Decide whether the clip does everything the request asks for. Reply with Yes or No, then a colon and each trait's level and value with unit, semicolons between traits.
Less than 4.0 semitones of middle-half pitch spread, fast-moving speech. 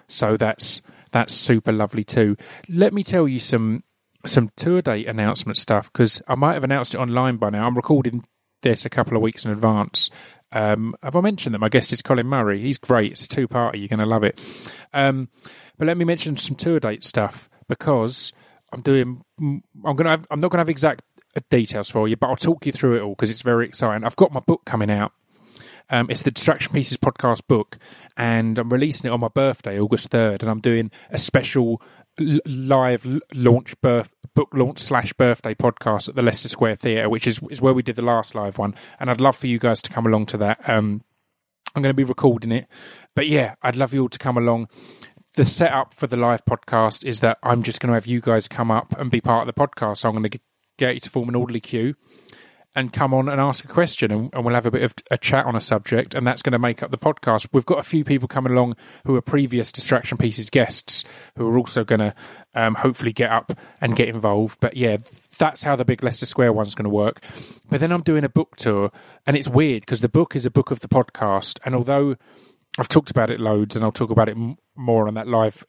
Yes: average, 3.4 semitones; fast, 235 wpm